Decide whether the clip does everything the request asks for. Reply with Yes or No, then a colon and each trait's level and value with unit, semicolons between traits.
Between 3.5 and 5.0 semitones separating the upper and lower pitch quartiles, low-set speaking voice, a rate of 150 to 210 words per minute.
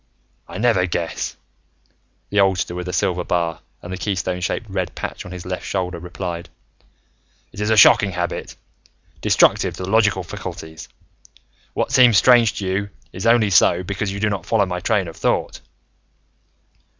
No: average, 2.7 semitones; very low, 95 Hz; average, 165 wpm